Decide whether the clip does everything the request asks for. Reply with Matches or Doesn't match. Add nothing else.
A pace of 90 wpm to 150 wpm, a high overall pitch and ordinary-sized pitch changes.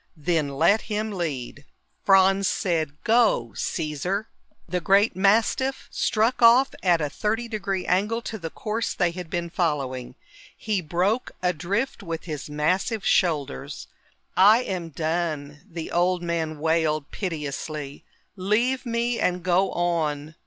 Doesn't match